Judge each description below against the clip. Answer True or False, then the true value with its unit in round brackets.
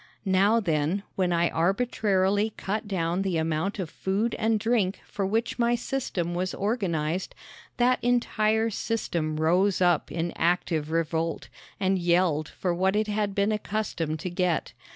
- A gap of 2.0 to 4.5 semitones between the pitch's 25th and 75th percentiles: True (4.0 semitones)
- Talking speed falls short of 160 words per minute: True (150 wpm)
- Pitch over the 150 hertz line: True (190 Hz)